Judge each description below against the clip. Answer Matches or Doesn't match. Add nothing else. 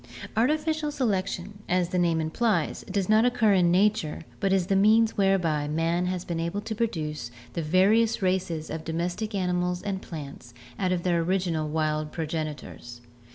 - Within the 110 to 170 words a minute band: Matches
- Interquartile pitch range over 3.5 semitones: Matches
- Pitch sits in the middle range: Matches